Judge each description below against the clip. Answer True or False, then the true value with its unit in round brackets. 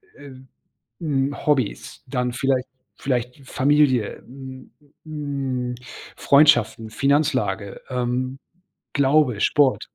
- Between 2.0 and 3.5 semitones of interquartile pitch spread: True (2.4 semitones)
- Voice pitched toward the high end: False (130 Hz)